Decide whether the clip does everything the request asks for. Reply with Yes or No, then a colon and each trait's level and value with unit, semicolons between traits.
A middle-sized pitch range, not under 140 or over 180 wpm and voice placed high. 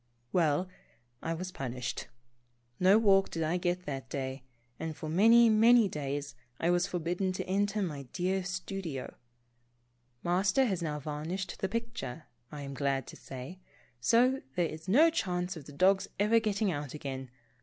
No: average, 5.0 semitones; average, 165 wpm; medium, 180 Hz